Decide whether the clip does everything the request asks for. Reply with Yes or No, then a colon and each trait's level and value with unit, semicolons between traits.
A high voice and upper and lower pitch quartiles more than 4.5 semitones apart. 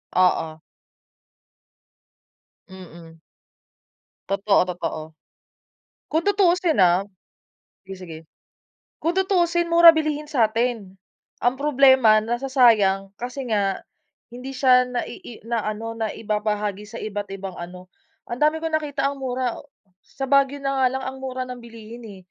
Yes: high, 240 Hz; wide, 5.4 semitones